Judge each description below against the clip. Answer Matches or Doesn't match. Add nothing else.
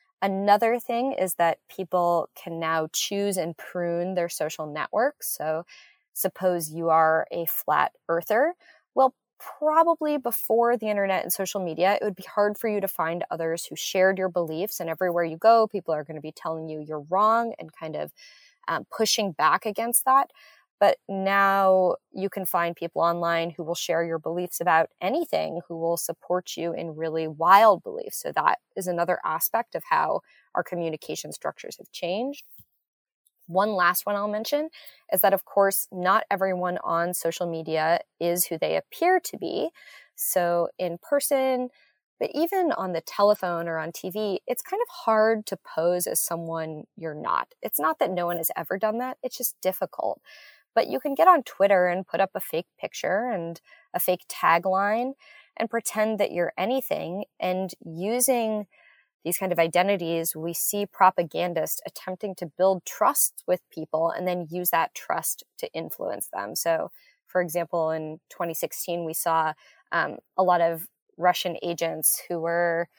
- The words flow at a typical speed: Matches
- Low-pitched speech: Doesn't match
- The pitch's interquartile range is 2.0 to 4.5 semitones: Doesn't match